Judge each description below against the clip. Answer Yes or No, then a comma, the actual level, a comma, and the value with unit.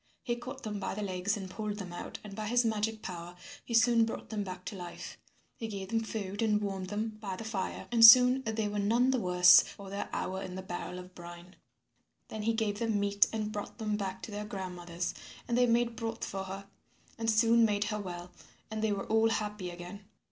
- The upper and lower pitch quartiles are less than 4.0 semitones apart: Yes, average, 2.9 semitones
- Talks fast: Yes, fast, 225 wpm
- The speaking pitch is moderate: No, high, 210 Hz